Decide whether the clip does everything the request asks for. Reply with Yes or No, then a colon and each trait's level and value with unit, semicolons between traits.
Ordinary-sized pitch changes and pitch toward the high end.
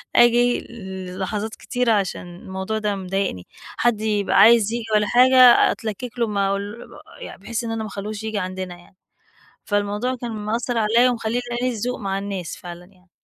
Yes: average, 3.4 semitones; high, 210 Hz